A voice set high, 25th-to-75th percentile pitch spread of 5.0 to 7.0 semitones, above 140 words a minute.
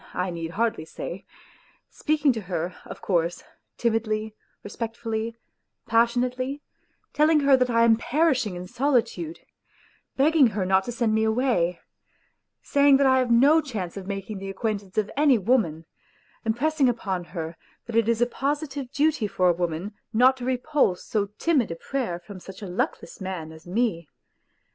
Yes: high, 225 Hz; wide, 5.6 semitones; average, 160 wpm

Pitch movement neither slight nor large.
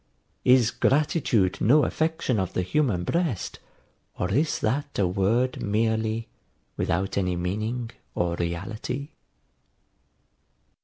No: wide, 5.7 semitones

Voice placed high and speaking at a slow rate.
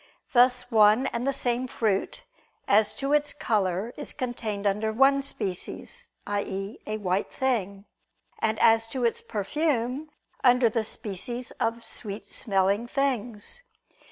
Yes: high, 230 Hz; slow, 130 wpm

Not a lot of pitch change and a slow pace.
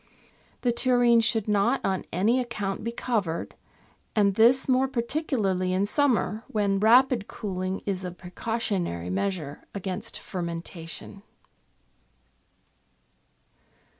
No: average, 4.2 semitones; slow, 105 wpm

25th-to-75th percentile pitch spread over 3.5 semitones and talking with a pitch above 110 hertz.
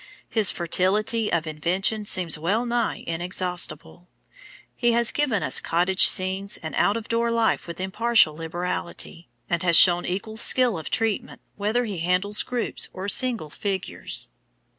Yes: average, 4.5 semitones; high, 190 Hz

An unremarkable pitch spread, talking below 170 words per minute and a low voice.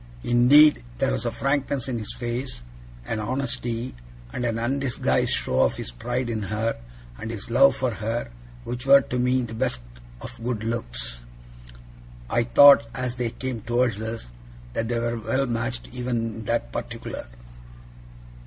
No: narrow, 2.1 semitones; average, 160 wpm; low, 120 Hz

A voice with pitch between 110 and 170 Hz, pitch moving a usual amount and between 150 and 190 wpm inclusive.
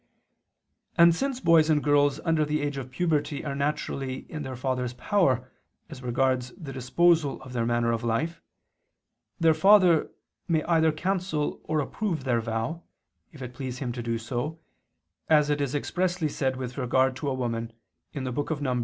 Yes: medium, 140 Hz; average, 4.1 semitones; average, 165 wpm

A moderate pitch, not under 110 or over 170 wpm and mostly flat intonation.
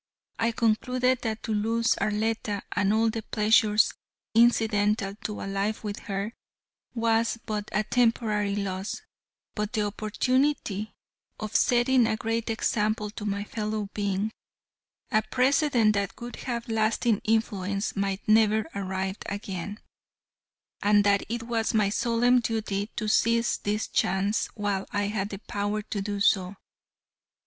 No: high, 215 Hz; average, 140 wpm; narrow, 1.9 semitones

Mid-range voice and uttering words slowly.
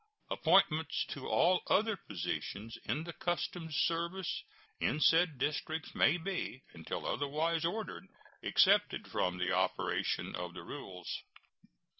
Yes: medium, 160 Hz; slow, 120 wpm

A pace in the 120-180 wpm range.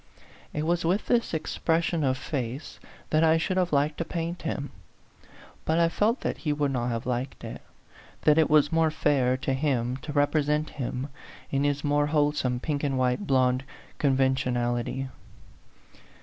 Yes: average, 165 wpm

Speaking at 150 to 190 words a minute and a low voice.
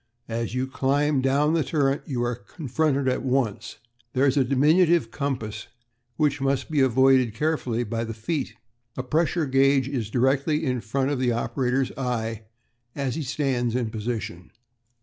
Yes: average, 170 wpm; low, 130 Hz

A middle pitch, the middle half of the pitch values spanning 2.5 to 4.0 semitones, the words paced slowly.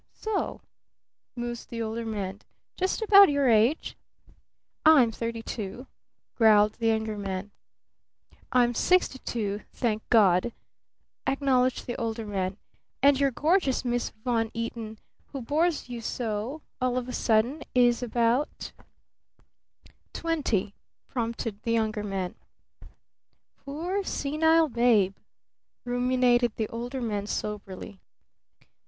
No: high, 235 Hz; average, 3.5 semitones; slow, 115 wpm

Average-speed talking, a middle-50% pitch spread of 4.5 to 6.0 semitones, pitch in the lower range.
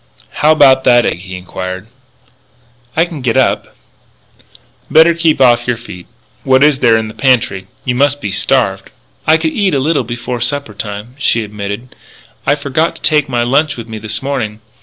Yes: average, 185 wpm; average, 4.8 semitones; low, 125 Hz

